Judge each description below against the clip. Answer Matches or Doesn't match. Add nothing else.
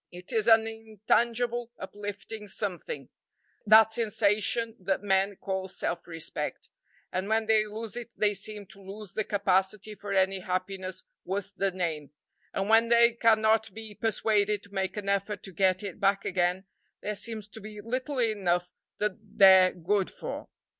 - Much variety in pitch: Doesn't match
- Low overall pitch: Doesn't match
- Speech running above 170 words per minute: Doesn't match